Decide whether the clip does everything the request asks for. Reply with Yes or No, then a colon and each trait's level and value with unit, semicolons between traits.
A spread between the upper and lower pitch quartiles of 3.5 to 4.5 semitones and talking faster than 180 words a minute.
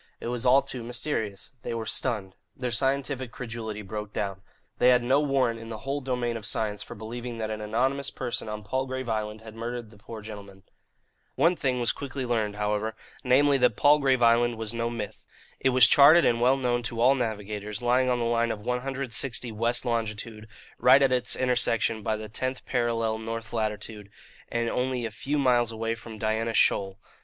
No: narrow, 2.6 semitones; average, 190 wpm